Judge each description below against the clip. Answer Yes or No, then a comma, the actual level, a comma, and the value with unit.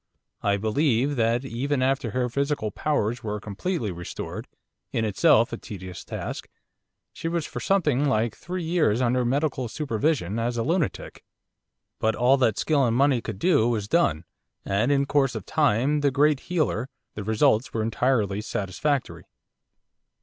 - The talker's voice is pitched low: Yes, low, 125 Hz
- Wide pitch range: No, average, 4.8 semitones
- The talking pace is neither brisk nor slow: Yes, average, 155 wpm